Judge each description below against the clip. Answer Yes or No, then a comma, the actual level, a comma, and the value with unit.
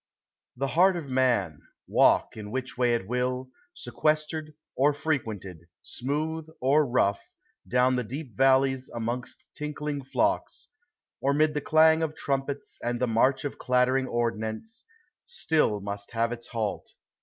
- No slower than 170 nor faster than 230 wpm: No, average, 145 wpm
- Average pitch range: Yes, average, 4.0 semitones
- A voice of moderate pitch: No, low, 130 Hz